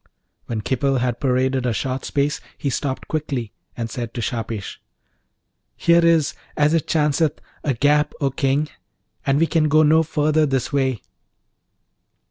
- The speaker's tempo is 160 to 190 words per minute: No, average, 150 wpm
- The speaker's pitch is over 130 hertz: Yes, medium, 140 Hz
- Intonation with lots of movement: No, average, 3.2 semitones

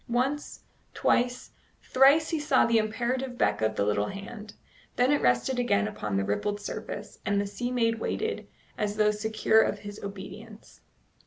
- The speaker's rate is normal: Yes, average, 165 wpm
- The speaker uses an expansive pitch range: No, average, 3.7 semitones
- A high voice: Yes, high, 215 Hz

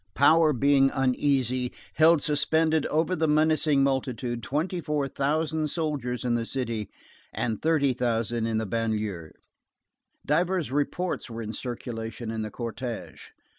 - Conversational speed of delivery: No, slow, 130 wpm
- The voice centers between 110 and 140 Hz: Yes, low, 135 Hz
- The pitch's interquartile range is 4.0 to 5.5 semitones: Yes, average, 4.8 semitones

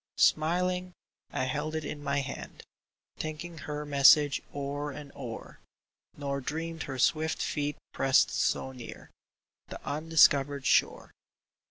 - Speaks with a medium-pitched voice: Yes, medium, 145 Hz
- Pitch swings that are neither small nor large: No, narrow, 2.1 semitones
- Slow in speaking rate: Yes, slow, 125 wpm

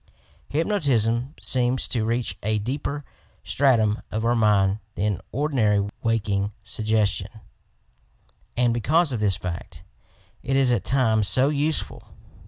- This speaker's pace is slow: Yes, slow, 125 wpm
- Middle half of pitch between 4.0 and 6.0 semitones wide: Yes, average, 4.3 semitones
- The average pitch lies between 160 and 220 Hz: No, low, 115 Hz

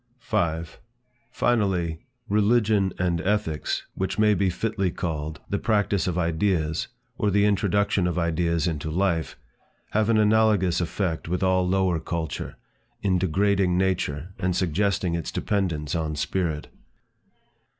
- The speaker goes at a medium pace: No, slow, 130 wpm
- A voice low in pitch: Yes, very low, 90 Hz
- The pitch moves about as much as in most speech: Yes, average, 3.5 semitones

